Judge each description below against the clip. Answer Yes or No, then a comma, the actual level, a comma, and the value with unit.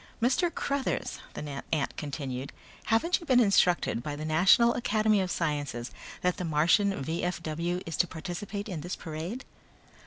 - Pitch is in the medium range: Yes, medium, 175 Hz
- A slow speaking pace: No, average, 150 wpm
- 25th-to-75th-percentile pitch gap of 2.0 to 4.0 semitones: No, wide, 5.6 semitones